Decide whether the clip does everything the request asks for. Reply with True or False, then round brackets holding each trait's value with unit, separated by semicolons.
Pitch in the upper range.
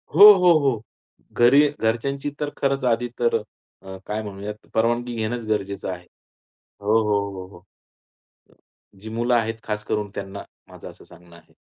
False (110 Hz)